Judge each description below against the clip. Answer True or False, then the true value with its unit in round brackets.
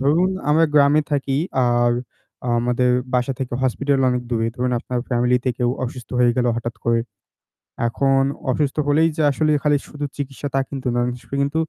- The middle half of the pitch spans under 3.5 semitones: True (2.6 semitones)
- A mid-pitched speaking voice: False (130 Hz)